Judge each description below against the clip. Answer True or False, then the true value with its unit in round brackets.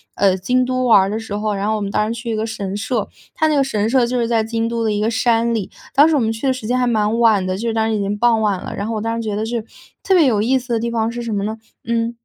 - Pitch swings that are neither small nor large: False (2.1 semitones)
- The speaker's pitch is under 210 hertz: False (225 Hz)